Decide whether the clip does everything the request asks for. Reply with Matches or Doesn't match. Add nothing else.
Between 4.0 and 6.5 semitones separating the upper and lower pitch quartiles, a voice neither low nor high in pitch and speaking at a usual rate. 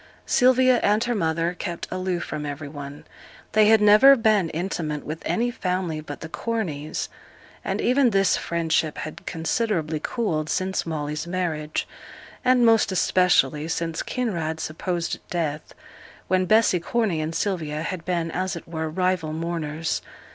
Matches